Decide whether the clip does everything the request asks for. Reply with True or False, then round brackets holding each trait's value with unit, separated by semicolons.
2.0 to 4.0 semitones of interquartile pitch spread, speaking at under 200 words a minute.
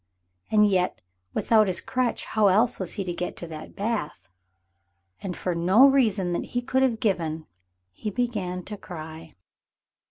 False (4.4 semitones; 160 wpm)